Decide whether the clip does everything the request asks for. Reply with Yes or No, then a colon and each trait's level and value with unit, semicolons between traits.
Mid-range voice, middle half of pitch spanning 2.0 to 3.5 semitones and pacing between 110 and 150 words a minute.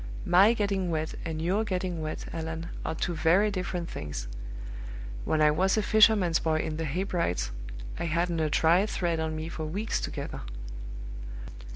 No: medium, 170 Hz; average, 3.1 semitones; average, 165 wpm